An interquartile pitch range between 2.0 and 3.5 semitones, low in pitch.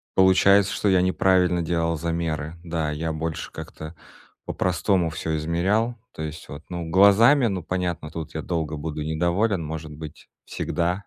Yes: average, 2.9 semitones; very low, 85 Hz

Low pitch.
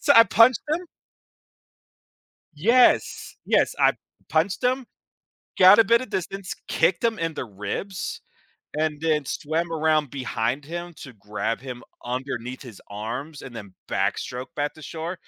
No: medium, 155 Hz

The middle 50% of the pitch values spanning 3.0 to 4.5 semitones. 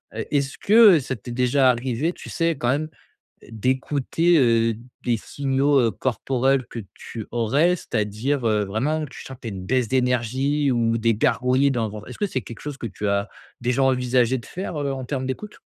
Yes: average, 3.3 semitones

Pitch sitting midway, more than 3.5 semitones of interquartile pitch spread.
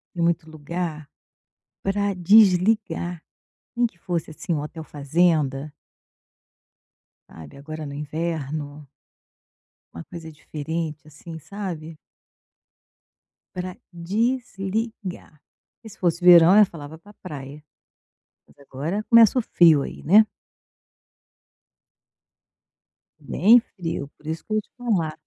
Yes: medium, 170 Hz; average, 4.2 semitones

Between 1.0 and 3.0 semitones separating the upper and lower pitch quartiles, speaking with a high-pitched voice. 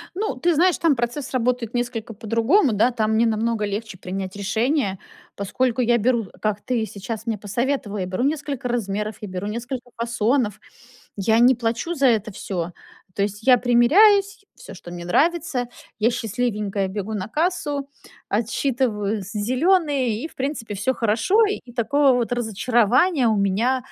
No: average, 3.9 semitones; high, 235 Hz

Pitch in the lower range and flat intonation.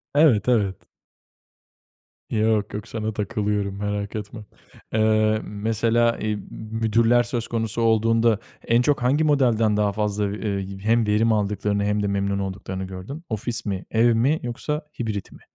Yes: low, 110 Hz; narrow, 2.1 semitones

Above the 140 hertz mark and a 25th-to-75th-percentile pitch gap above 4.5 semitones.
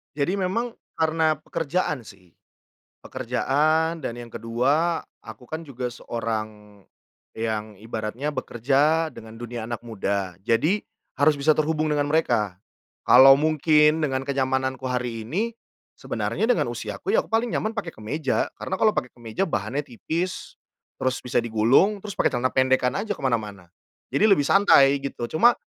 No: low, 135 Hz; wide, 5.5 semitones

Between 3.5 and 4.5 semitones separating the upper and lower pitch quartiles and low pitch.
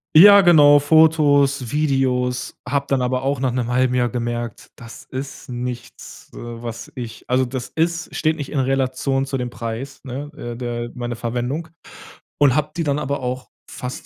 No: average, 2.7 semitones; low, 130 Hz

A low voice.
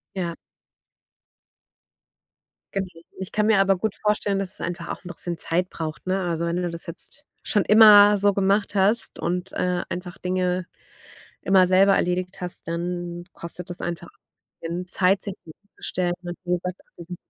No: medium, 180 Hz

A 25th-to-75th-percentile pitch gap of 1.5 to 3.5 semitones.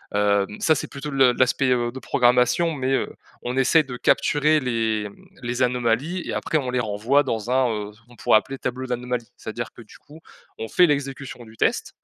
Yes: average, 2.8 semitones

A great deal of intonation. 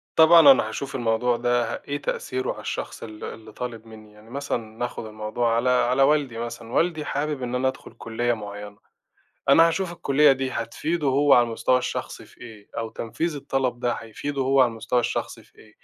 No: average, 3.5 semitones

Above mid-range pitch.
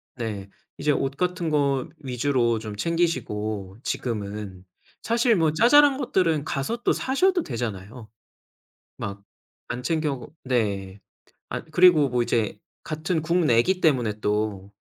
No: low, 130 Hz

